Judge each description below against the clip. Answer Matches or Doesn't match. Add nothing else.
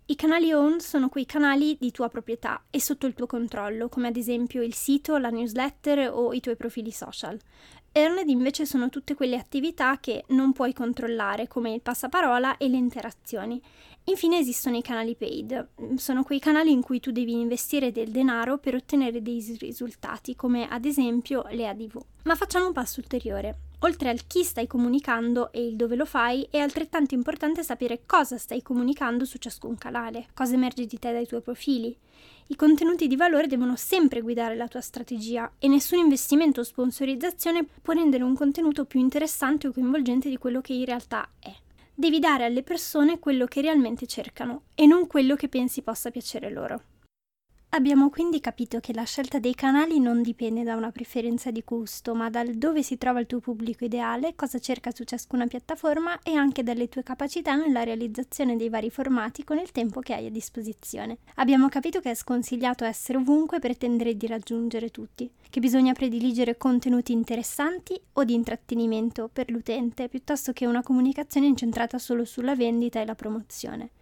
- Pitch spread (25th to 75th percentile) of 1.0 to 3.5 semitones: Matches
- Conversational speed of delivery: Doesn't match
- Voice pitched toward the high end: Matches